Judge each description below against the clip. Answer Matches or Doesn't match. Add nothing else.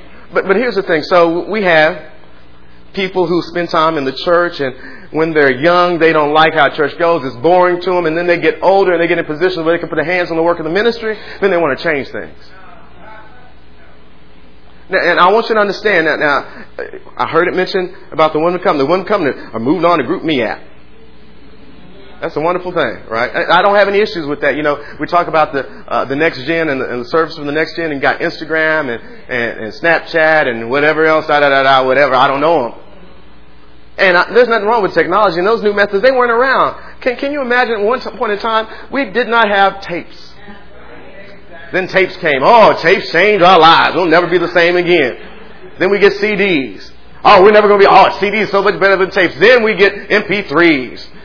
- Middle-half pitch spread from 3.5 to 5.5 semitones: Matches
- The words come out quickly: Matches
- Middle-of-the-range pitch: Matches